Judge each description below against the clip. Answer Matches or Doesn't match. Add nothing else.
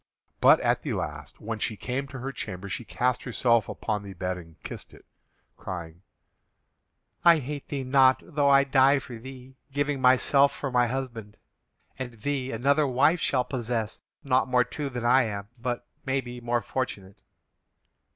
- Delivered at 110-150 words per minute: Doesn't match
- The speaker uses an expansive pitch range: Doesn't match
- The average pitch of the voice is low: Matches